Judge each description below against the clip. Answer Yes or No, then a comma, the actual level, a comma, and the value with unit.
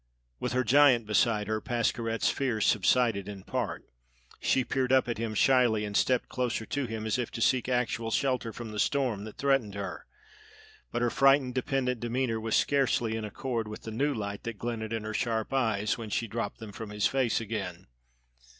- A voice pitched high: No, low, 115 Hz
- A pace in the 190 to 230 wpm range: Yes, average, 195 wpm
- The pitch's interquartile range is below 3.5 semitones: Yes, average, 2.8 semitones